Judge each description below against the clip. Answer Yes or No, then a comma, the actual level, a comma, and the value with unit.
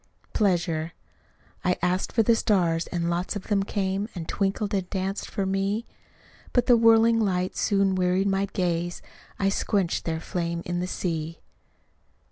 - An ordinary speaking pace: Yes, average, 155 wpm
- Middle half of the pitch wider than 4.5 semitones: No, narrow, 2.5 semitones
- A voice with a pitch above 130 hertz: Yes, high, 190 Hz